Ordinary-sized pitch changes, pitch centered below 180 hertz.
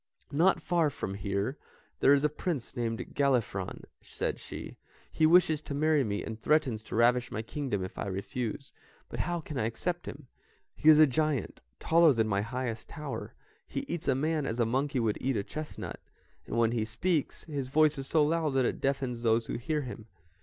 Yes: average, 5.0 semitones; low, 135 Hz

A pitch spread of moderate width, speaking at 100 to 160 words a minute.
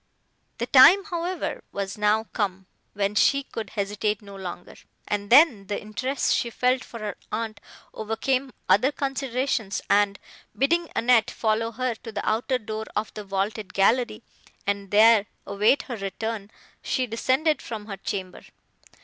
Yes: average, 3.9 semitones; average, 150 wpm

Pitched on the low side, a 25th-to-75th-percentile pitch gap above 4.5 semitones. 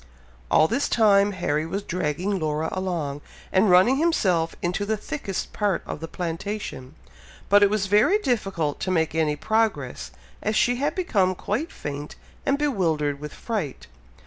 No: high, 190 Hz; average, 5.1 semitones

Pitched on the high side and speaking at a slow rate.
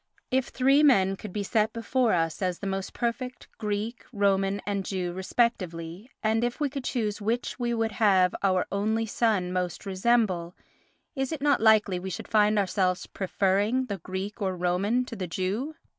No: high, 205 Hz; average, 175 wpm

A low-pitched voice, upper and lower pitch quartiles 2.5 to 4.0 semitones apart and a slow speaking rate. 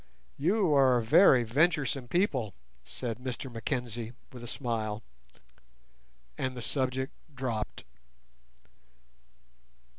Yes: low, 125 Hz; average, 2.9 semitones; slow, 90 wpm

